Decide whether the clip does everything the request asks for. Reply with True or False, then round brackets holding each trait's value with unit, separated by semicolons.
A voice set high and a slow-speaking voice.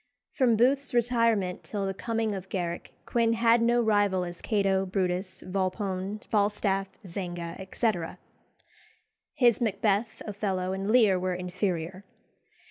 True (195 Hz; 125 wpm)